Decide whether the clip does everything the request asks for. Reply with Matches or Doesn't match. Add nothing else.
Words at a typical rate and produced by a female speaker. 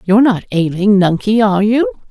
Matches